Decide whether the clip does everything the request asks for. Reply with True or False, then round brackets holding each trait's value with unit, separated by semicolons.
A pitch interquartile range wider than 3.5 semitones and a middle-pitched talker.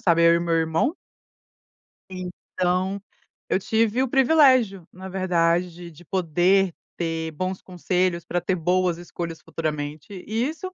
False (2.4 semitones; 180 Hz)